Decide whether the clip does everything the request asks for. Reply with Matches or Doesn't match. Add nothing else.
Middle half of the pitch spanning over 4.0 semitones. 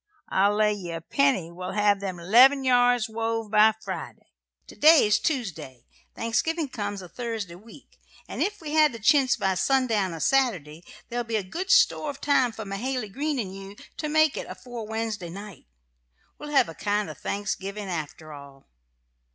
Matches